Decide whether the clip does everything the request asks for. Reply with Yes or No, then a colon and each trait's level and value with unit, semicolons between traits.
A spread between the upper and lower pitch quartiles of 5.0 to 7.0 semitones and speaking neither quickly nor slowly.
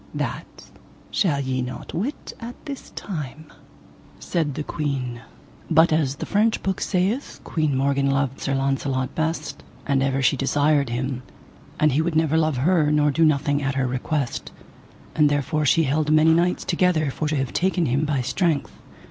No: average, 2.9 semitones; average, 175 wpm